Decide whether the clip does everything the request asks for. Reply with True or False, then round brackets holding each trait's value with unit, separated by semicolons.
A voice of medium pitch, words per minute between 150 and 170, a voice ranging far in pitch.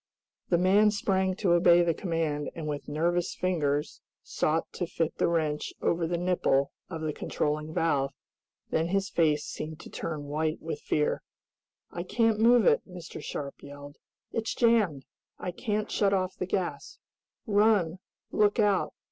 False (170 Hz; 155 wpm; 4.1 semitones)